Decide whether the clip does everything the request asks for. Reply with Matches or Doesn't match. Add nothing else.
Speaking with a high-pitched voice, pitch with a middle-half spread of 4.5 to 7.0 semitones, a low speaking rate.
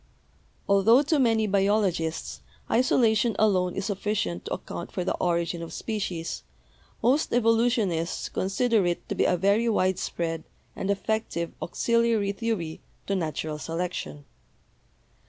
Matches